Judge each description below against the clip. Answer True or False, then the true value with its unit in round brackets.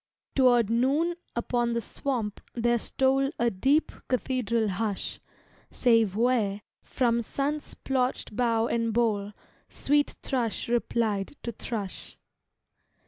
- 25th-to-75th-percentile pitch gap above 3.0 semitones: False (2.6 semitones)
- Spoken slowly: True (110 wpm)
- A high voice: True (235 Hz)